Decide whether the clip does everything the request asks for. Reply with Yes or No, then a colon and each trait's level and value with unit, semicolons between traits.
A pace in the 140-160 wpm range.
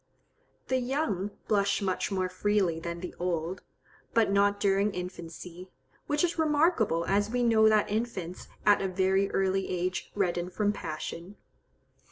Yes: average, 145 wpm